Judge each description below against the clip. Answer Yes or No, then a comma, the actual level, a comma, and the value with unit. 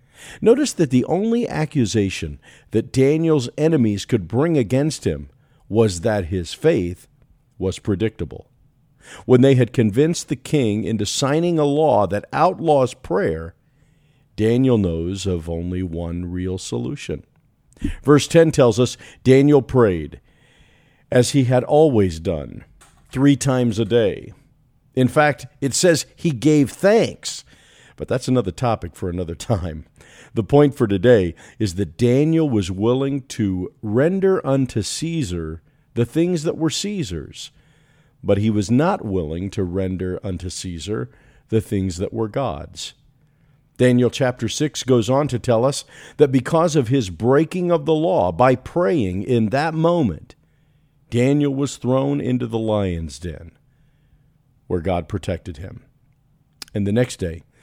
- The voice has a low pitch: Yes, low, 125 Hz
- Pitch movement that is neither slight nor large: No, wide, 6.5 semitones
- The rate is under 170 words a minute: Yes, average, 140 wpm